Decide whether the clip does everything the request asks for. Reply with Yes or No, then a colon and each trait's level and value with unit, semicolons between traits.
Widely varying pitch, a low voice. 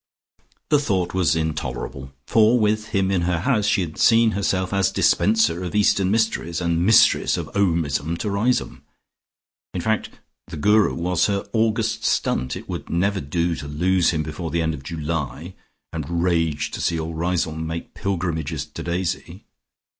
No: average, 3.8 semitones; very low, 90 Hz